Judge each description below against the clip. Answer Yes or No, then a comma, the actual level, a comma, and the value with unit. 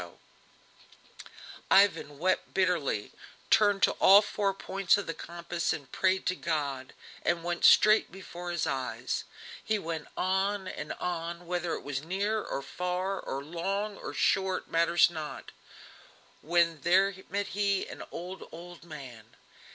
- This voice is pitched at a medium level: Yes, medium, 175 Hz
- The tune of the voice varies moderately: Yes, average, 3.1 semitones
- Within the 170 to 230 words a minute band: No, average, 145 wpm